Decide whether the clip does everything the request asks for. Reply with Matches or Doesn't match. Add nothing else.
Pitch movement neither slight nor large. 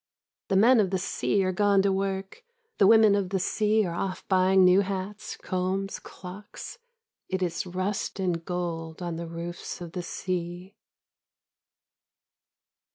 Doesn't match